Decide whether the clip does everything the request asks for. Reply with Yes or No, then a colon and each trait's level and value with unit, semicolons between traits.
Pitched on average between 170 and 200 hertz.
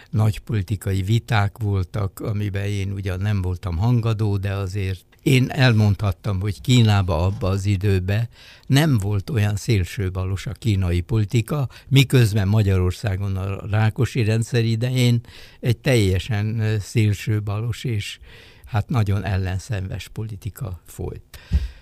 No: low, 105 Hz